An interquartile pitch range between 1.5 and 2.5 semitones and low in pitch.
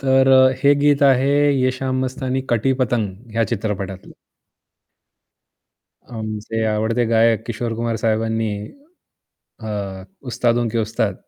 No: average, 2.9 semitones; low, 115 Hz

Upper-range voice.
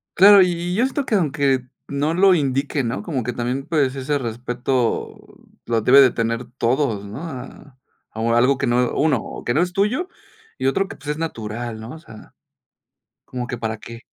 No: low, 135 Hz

